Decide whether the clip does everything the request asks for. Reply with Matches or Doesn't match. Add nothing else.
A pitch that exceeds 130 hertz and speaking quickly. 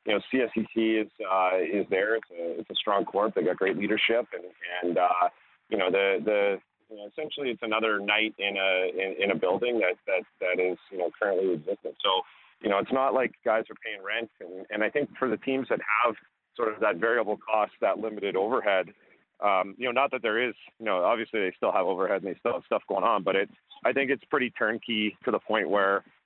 Doesn't match